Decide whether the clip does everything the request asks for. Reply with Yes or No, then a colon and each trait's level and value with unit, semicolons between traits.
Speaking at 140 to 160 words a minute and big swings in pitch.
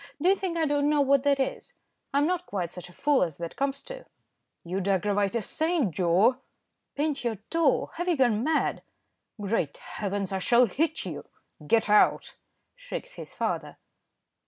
No: average, 175 wpm; wide, 7.9 semitones